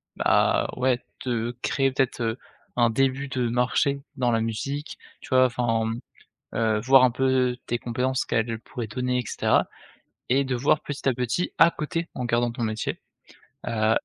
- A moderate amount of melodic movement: No, narrow, 2.2 semitones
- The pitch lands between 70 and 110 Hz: No, low, 125 Hz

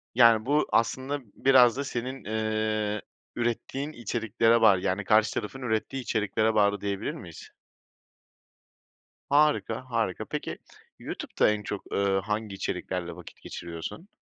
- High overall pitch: No, low, 110 Hz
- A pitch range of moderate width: Yes, average, 3.2 semitones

